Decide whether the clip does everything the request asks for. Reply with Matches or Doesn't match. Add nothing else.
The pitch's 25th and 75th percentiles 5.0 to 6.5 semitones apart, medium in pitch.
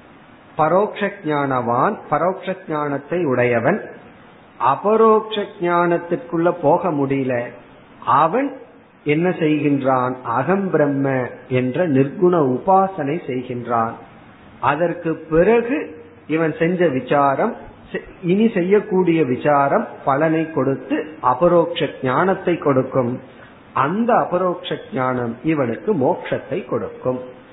Matches